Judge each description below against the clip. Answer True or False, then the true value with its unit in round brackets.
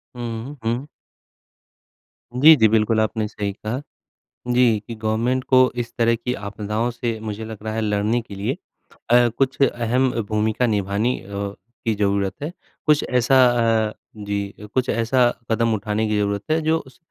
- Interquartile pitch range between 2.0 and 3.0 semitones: True (2.6 semitones)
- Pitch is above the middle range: False (115 Hz)